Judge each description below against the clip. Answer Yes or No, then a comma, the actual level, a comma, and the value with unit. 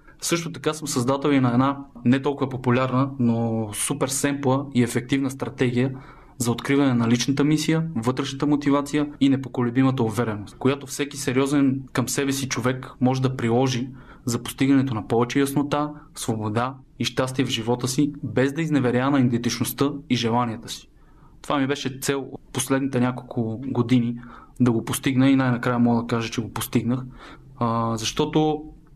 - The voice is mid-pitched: No, low, 130 Hz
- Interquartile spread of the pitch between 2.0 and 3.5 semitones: Yes, narrow, 2.4 semitones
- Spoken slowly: No, average, 155 wpm